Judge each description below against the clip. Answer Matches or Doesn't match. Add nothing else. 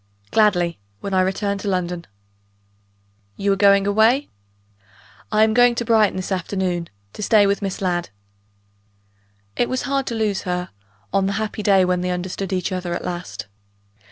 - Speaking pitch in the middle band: Doesn't match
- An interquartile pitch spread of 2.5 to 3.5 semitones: Matches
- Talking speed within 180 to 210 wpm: Doesn't match